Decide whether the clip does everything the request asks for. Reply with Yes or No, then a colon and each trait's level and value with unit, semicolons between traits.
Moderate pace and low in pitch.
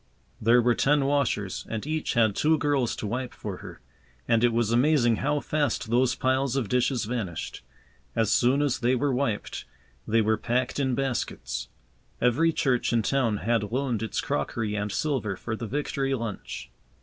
Yes: average, 175 wpm; low, 120 Hz